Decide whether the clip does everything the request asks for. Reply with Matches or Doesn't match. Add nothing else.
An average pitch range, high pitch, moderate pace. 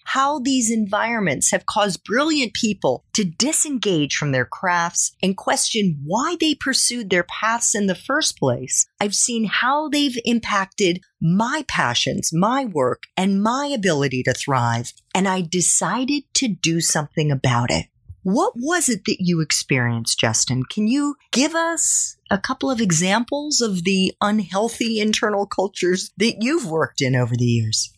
Doesn't match